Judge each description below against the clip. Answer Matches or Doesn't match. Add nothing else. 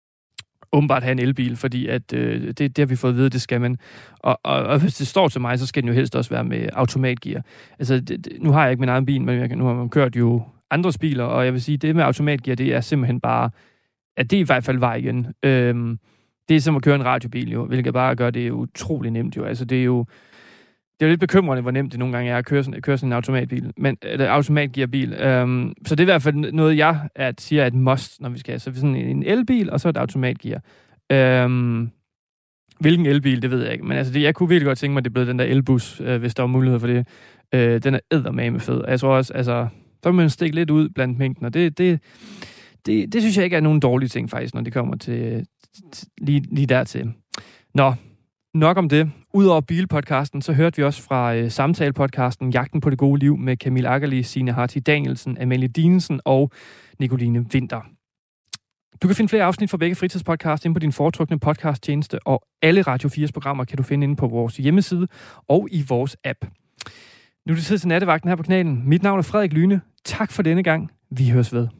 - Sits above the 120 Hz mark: Matches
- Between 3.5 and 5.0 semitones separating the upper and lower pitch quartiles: Matches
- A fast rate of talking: Matches